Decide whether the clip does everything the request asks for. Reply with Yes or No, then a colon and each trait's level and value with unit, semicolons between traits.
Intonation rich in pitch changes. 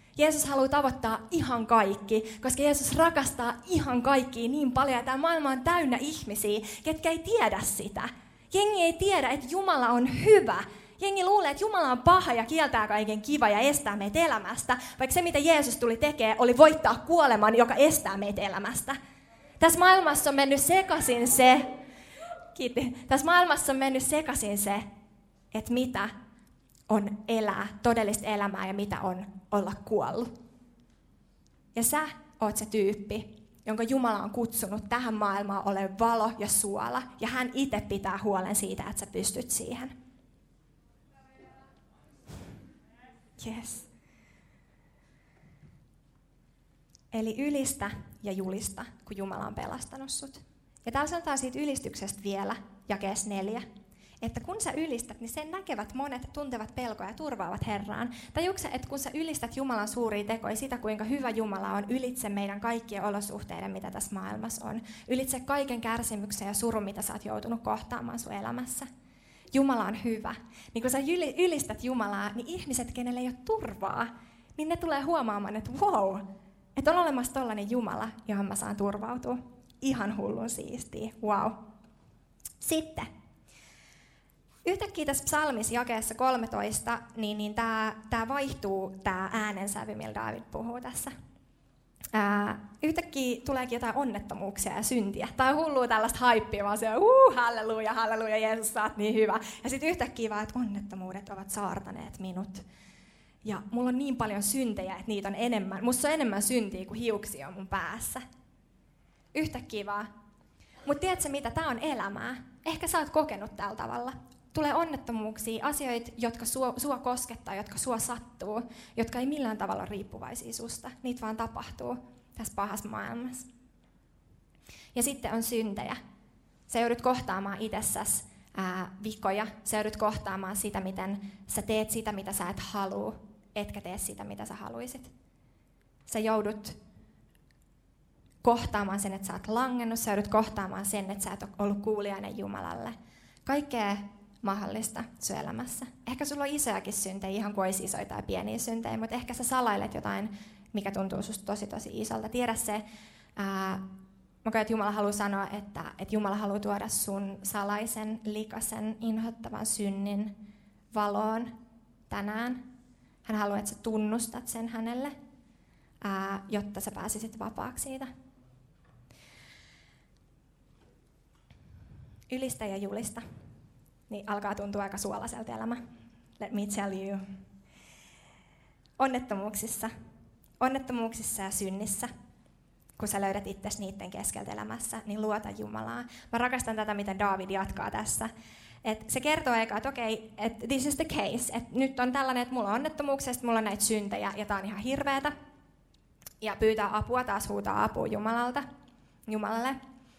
No: average, 4.0 semitones